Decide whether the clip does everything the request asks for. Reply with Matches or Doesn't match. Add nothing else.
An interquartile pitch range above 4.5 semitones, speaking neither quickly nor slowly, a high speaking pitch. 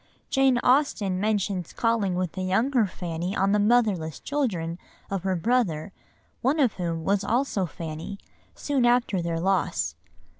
Matches